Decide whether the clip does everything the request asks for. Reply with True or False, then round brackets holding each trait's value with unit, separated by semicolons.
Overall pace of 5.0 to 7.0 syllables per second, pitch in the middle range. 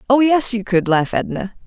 False (5.7 syllables/s; 220 Hz)